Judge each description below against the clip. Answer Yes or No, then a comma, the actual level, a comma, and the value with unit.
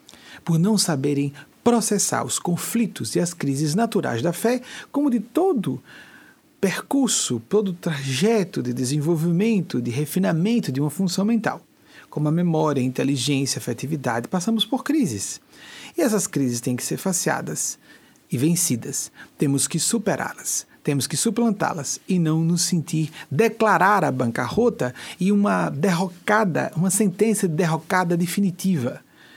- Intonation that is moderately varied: No, wide, 6.5 semitones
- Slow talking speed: No, average, 135 wpm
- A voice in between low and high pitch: Yes, medium, 175 Hz